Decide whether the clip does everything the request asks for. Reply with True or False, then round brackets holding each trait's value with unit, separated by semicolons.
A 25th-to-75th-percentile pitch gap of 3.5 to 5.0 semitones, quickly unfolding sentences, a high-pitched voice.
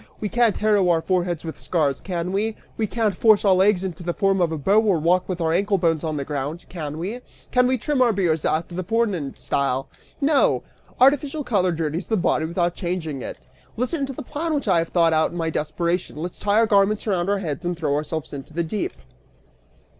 False (4.7 semitones; 225 wpm; 180 Hz)